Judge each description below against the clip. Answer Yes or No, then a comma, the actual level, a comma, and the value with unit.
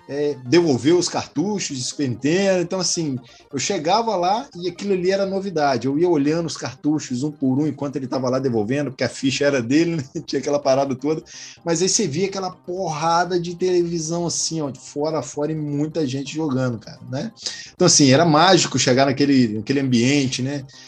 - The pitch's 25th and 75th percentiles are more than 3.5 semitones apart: Yes, average, 4.0 semitones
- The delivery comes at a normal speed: No, fast, 195 wpm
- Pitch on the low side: No, medium, 145 Hz